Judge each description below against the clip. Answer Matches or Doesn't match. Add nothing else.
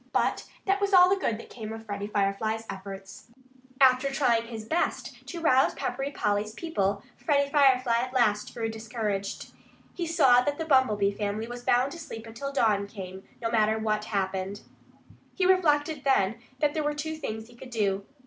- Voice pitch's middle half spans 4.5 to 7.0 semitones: Matches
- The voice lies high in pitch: Matches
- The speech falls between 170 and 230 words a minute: Matches